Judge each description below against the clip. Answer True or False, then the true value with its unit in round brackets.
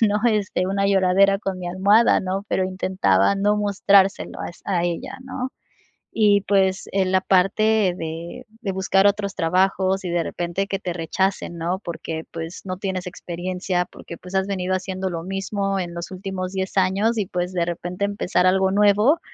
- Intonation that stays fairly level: True (1.7 semitones)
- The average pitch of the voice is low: False (190 Hz)